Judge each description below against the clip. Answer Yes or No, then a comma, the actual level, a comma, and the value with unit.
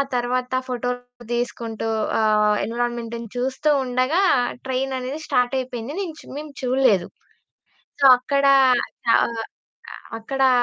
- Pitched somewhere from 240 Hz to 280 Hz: Yes, very high, 250 Hz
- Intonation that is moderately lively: No, narrow, 2.0 semitones